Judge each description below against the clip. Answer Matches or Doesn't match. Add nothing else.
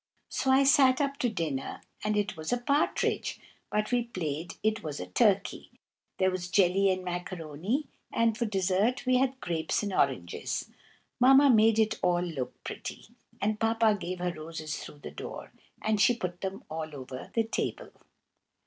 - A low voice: Doesn't match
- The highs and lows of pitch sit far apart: Matches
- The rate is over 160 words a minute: Matches